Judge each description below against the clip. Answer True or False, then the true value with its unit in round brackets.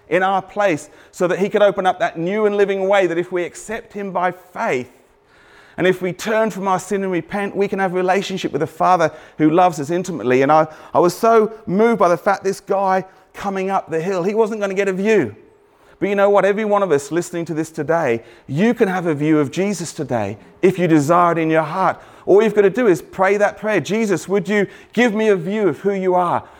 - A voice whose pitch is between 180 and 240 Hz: True (190 Hz)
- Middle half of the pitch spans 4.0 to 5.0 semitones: False (3.0 semitones)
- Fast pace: True (250 wpm)